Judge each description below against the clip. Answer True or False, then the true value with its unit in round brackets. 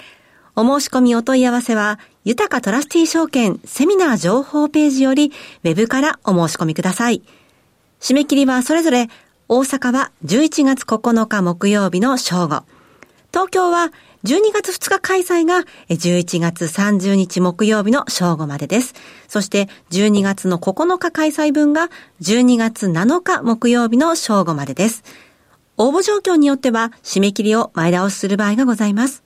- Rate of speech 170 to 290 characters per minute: True (280 characters per minute)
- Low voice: False (235 Hz)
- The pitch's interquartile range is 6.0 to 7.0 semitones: True (6.5 semitones)